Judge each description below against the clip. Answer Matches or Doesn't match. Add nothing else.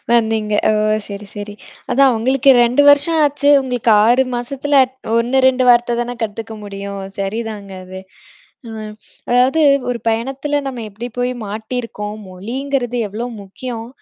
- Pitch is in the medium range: Doesn't match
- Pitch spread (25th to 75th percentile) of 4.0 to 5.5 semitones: Doesn't match